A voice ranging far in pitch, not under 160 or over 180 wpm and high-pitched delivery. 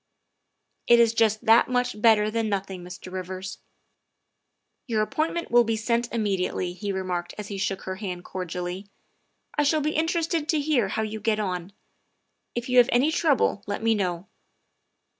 No: average, 4.2 semitones; average, 175 wpm; high, 215 Hz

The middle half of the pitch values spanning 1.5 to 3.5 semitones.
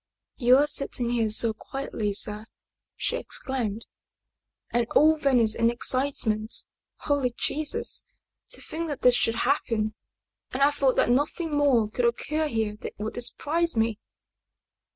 No: average, 4.4 semitones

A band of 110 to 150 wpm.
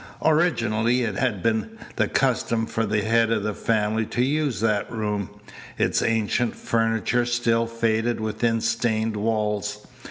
Yes: average, 140 wpm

